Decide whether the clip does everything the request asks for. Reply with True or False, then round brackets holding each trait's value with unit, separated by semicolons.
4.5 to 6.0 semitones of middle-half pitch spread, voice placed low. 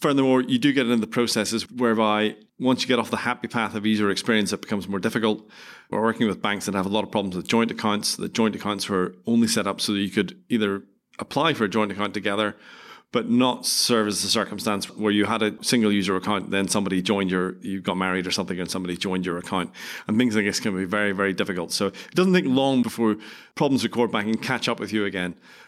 False (2.8 semitones; 105 Hz)